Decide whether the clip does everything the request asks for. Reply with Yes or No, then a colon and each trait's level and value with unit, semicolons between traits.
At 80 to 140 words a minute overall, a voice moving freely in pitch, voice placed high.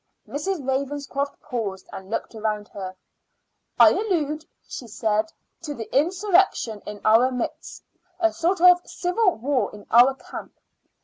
Yes: slow, 135 wpm; wide, 7.4 semitones; very high, 270 Hz